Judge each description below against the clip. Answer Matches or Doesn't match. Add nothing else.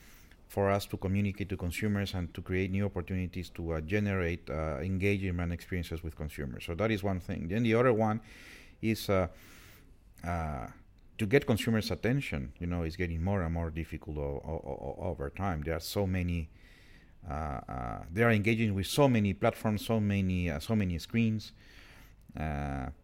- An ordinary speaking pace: Matches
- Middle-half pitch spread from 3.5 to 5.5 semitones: Matches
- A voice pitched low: Matches